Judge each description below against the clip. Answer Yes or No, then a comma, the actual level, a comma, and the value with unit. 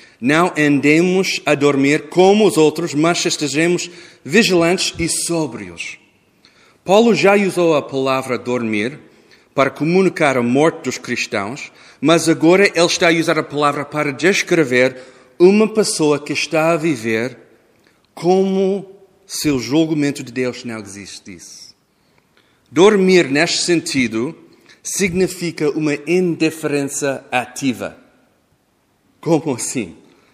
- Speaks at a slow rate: Yes, slow, 115 wpm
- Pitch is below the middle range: No, medium, 160 Hz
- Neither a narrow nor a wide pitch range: Yes, average, 4.0 semitones